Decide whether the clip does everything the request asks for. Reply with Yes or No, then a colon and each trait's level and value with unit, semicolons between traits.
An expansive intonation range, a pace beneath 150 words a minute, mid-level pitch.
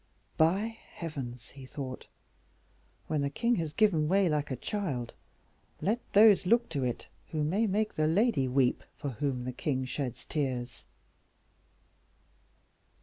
Yes: wide, 7.2 semitones; average, 140 wpm; medium, 150 Hz